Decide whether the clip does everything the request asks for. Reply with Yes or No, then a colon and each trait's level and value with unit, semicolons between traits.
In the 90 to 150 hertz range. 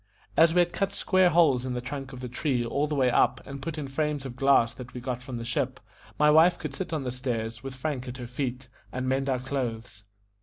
Yes: low, 135 Hz